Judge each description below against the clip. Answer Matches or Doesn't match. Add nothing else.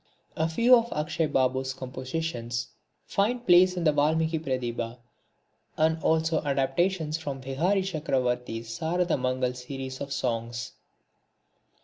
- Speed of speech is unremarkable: Doesn't match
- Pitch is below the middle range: Doesn't match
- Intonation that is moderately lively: Matches